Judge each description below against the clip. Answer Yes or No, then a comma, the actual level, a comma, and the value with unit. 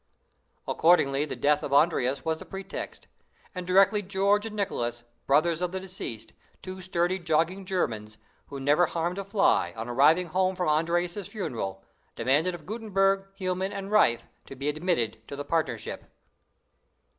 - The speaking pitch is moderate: Yes, medium, 175 Hz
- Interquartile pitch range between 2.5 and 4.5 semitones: No, average, 5.1 semitones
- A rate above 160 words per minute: No, average, 155 wpm